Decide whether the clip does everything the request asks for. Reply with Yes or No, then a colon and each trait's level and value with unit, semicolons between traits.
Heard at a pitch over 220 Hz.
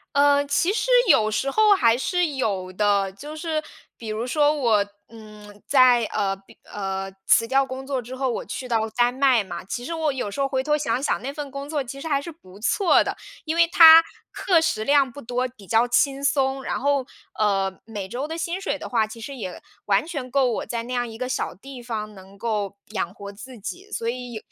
Yes: very high, 250 Hz